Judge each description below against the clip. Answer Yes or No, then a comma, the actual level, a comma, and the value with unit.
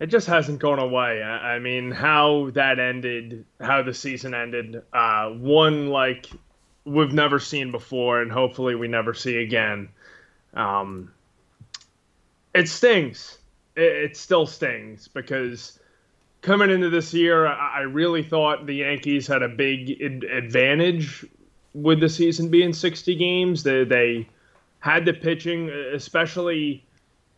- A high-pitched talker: No, medium, 140 Hz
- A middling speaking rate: No, slow, 130 wpm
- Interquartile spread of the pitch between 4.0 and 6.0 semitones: Yes, average, 4.9 semitones